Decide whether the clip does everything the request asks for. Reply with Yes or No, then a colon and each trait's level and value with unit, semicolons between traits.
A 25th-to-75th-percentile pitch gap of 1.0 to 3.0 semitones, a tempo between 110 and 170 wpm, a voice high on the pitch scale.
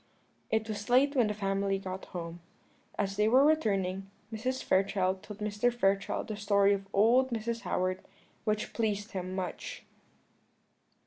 Yes: narrow, 2.5 semitones; average, 145 wpm; high, 205 Hz